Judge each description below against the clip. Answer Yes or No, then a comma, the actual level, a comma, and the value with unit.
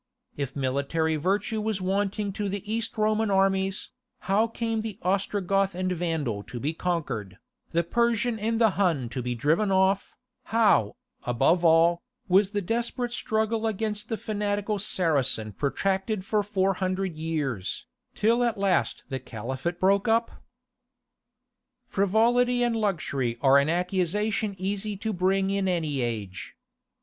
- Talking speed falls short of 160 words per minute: Yes, average, 140 wpm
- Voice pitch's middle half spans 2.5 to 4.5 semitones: No, average, 4.9 semitones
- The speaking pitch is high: Yes, high, 195 Hz